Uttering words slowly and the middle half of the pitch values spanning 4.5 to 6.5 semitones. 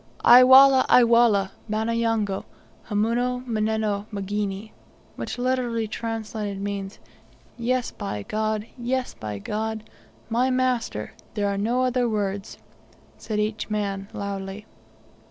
No: slow, 120 wpm; average, 3.0 semitones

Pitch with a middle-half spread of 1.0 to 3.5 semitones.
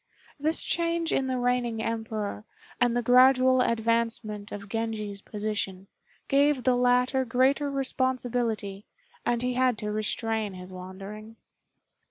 Yes: average, 3.2 semitones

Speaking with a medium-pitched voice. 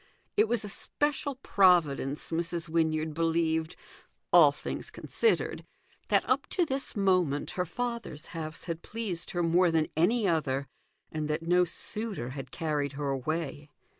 Yes: medium, 165 Hz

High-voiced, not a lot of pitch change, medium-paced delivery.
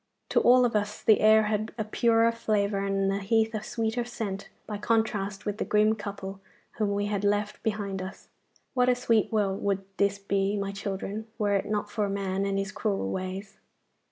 Yes: high, 205 Hz; narrow, 1.8 semitones; average, 195 wpm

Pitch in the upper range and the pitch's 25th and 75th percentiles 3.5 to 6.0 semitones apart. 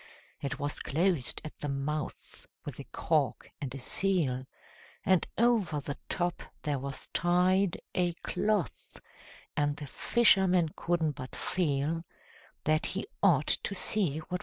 No: medium, 160 Hz; average, 4.5 semitones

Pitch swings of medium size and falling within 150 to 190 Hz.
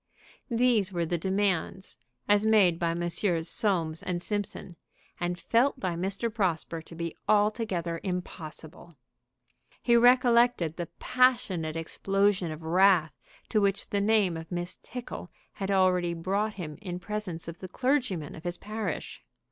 Yes: average, 3.9 semitones; medium, 185 Hz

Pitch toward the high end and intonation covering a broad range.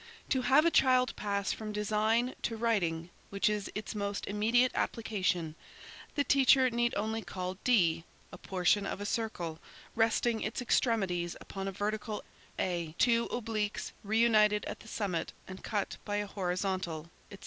No: high, 210 Hz; average, 3.4 semitones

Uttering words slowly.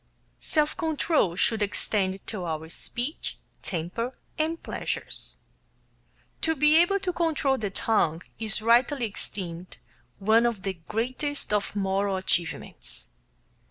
Yes: slow, 120 wpm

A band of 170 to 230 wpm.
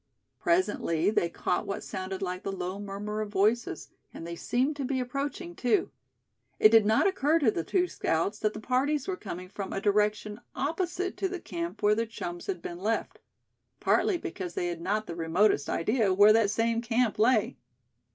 Yes: average, 190 wpm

